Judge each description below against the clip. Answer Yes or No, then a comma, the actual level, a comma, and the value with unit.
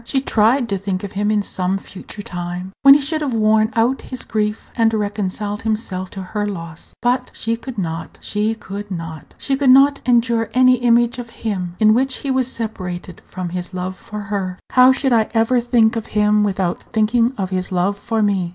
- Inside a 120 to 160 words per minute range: No, fast, 205 wpm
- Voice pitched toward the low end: No, high, 215 Hz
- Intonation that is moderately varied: Yes, average, 4.0 semitones